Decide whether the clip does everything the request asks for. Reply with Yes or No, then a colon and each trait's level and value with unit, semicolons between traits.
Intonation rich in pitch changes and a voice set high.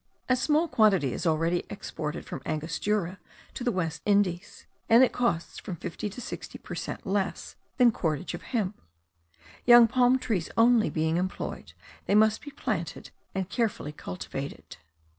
Yes: wide, 6.1 semitones; high, 200 Hz